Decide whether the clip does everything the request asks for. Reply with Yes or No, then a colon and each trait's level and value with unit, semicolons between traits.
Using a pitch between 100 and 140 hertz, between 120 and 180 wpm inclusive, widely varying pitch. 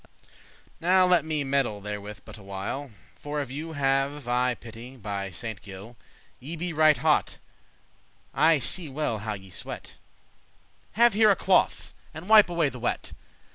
Yes: low, 135 Hz; average, 160 wpm; wide, 6.6 semitones